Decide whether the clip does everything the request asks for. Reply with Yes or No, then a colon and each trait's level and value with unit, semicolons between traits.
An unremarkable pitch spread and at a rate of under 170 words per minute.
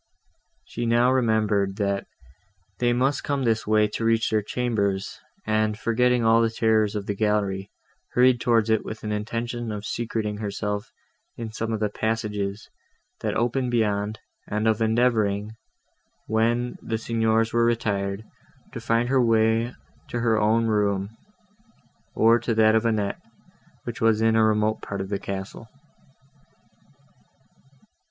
No: narrow, 1.8 semitones; average, 145 wpm